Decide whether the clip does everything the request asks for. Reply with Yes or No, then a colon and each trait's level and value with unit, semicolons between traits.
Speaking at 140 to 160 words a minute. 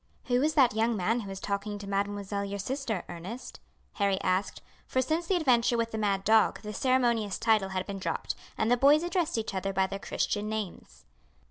No: fast, 205 wpm